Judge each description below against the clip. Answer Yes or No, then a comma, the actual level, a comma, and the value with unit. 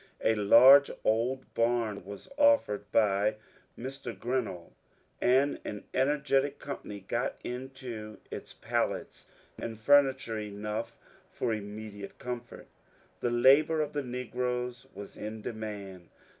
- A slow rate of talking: Yes, slow, 115 wpm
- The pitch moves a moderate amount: Yes, average, 3.8 semitones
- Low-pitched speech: Yes, low, 120 Hz